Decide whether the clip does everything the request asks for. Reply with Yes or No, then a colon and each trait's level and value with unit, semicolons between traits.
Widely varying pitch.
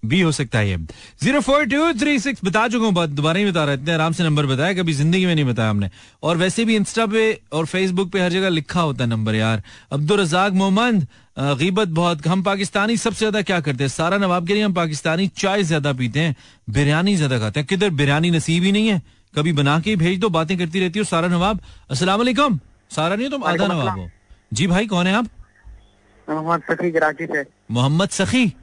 Yes: wide, 5.7 semitones